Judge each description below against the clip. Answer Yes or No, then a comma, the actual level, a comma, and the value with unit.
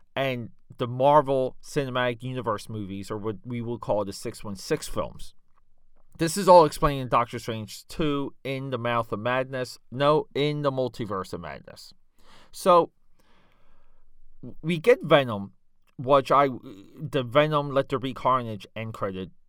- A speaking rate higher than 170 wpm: No, average, 145 wpm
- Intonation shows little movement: No, average, 3.5 semitones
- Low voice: Yes, low, 130 Hz